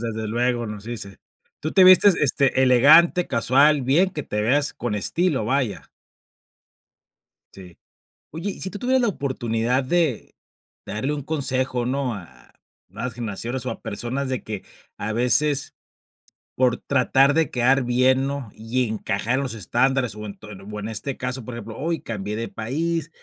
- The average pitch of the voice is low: Yes, low, 125 Hz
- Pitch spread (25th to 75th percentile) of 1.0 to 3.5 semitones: No, average, 4.1 semitones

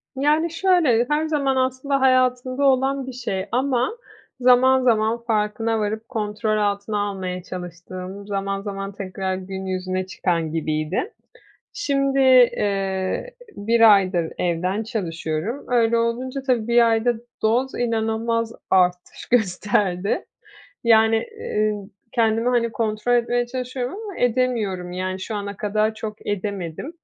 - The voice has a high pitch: Yes, high, 220 Hz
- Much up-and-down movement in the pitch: No, average, 4.4 semitones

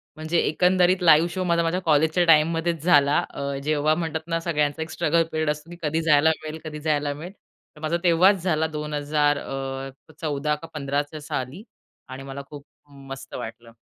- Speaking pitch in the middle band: Yes, medium, 155 Hz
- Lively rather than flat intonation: No, narrow, 2.4 semitones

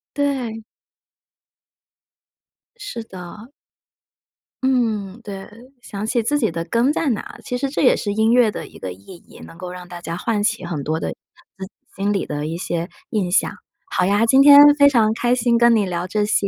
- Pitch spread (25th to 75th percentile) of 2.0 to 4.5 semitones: No, average, 5.0 semitones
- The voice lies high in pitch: Yes, high, 210 Hz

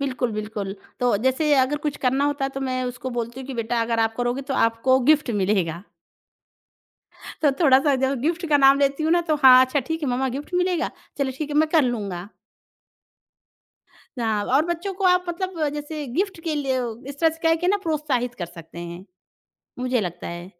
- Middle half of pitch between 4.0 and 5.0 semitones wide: Yes, average, 4.6 semitones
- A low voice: No, very high, 265 Hz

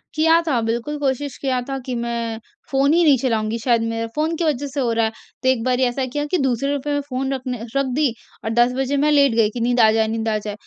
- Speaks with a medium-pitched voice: No, very high, 255 Hz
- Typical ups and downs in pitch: Yes, average, 3.6 semitones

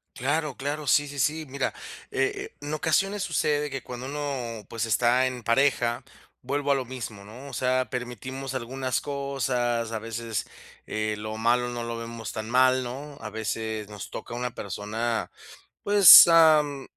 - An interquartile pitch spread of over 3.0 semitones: Yes, average, 3.7 semitones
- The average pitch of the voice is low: Yes, low, 130 Hz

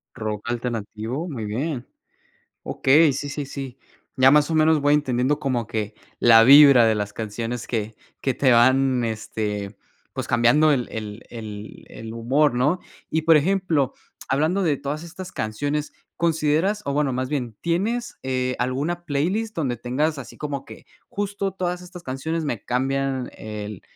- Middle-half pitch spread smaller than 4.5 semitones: No, average, 4.8 semitones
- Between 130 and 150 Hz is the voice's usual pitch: Yes, low, 135 Hz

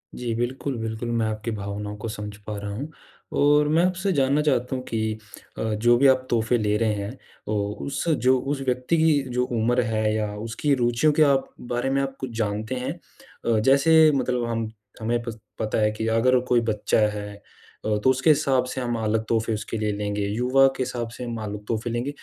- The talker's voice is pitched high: No, low, 120 Hz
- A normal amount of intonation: Yes, average, 3.4 semitones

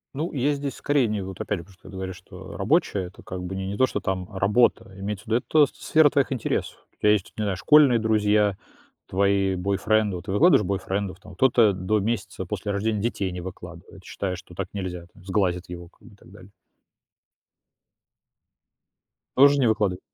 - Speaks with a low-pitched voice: Yes, low, 100 Hz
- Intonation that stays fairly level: No, average, 3.2 semitones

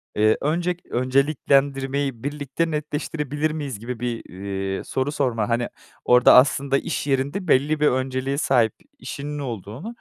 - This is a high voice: No, low, 135 Hz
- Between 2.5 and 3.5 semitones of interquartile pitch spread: Yes, average, 3.2 semitones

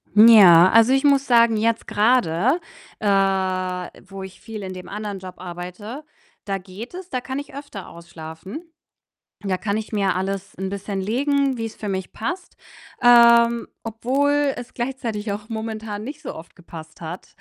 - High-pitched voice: Yes, high, 215 Hz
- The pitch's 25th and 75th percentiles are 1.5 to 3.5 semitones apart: No, average, 4.3 semitones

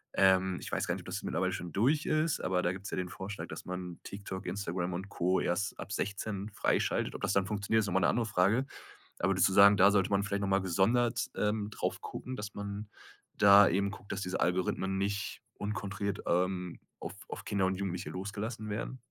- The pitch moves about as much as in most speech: No, narrow, 1.7 semitones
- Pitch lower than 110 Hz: Yes, low, 100 Hz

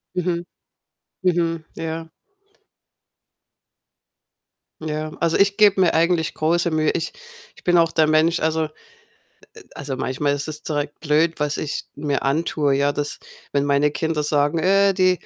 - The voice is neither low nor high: Yes, medium, 160 Hz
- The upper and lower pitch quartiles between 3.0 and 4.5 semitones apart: No, narrow, 2.4 semitones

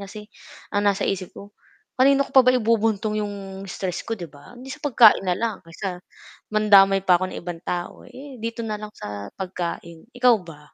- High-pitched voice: Yes, high, 205 Hz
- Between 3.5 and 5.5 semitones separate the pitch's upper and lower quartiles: Yes, average, 4.2 semitones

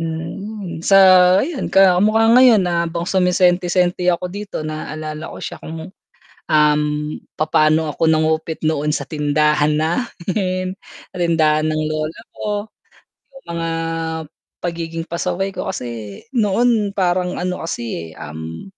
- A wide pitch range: No, average, 3.3 semitones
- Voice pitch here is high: No, medium, 170 Hz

